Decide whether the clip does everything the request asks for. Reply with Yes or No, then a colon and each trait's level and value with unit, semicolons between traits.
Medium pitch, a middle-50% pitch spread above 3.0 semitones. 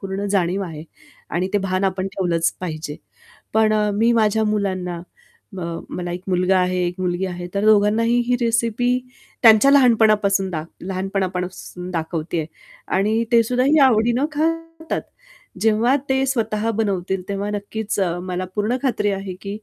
No: high, 200 Hz; average, 3.7 semitones